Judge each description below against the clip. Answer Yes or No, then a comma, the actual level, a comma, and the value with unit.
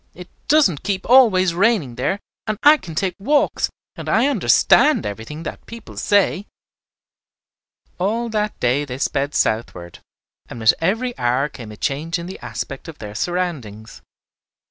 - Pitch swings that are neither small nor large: No, wide, 8.9 semitones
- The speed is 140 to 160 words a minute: Yes, average, 150 wpm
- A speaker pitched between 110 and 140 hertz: No, medium, 170 Hz